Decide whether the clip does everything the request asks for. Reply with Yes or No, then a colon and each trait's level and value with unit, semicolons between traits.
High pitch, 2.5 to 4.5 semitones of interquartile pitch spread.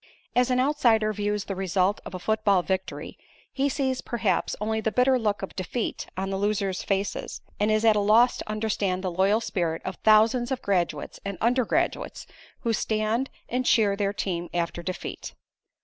Yes: high, 210 Hz; average, 3.0 semitones